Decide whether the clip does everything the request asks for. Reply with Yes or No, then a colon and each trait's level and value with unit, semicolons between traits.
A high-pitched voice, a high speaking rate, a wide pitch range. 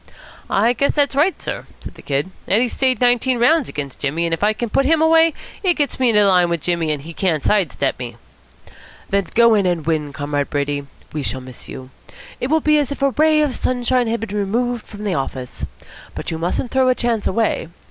Yes: high, 210 Hz; fast, 225 wpm; wide, 8.3 semitones